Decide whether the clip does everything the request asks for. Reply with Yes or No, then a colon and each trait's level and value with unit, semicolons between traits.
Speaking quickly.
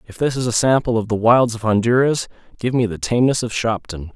Yes: fast, 230 wpm